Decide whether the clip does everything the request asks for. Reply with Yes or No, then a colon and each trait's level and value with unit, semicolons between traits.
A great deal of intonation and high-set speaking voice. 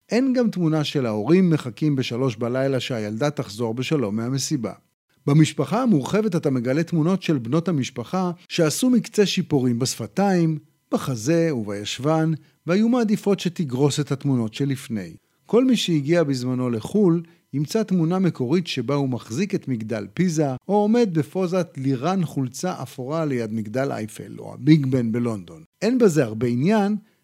No: wide, 6.0 semitones; medium, 155 Hz